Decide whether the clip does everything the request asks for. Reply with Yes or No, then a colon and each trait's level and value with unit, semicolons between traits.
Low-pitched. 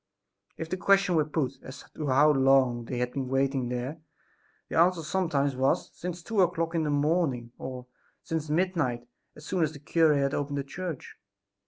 No: medium, 145 Hz